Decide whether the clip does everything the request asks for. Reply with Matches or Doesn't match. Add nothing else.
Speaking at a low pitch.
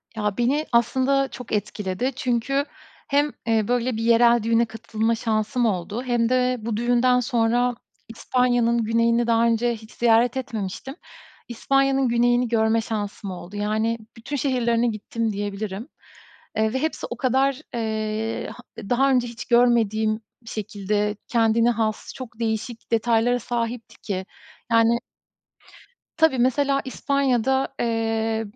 Doesn't match